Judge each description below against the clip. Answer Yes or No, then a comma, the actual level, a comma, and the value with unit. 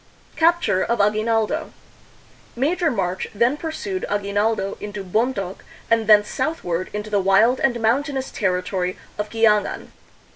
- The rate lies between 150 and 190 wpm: No, average, 140 wpm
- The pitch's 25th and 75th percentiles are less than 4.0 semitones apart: No, average, 4.6 semitones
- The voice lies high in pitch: Yes, high, 220 Hz